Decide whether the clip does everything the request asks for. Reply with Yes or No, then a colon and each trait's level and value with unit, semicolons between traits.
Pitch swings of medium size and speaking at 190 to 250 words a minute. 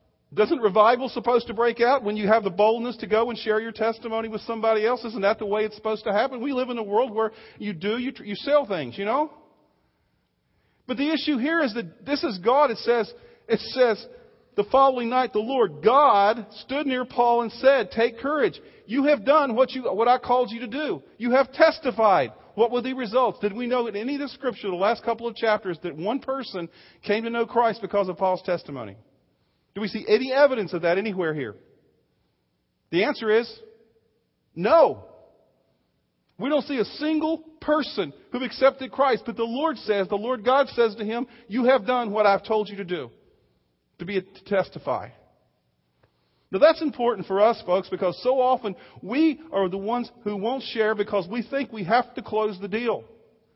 Yes: average, 3.8 semitones; average, 200 wpm